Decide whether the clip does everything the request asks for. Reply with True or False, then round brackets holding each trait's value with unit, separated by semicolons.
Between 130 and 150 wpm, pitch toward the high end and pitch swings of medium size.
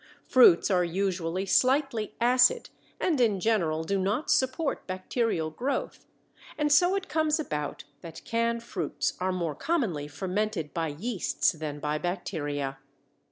False (135 wpm; 195 Hz; 7.4 semitones)